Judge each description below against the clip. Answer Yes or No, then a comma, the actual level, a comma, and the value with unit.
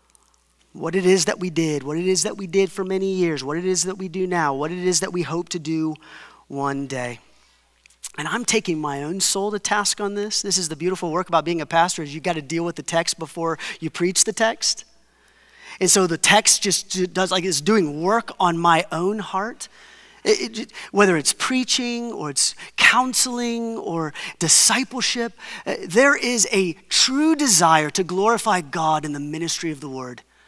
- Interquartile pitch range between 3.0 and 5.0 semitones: Yes, average, 4.5 semitones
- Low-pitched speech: No, medium, 185 Hz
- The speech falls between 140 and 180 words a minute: No, fast, 205 wpm